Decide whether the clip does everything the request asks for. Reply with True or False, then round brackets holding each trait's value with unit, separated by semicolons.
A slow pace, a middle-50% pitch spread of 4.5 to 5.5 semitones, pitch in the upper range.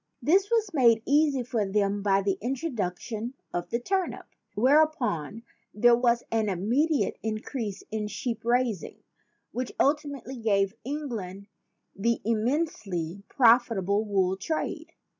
True (120 wpm; 5.1 semitones; 230 Hz)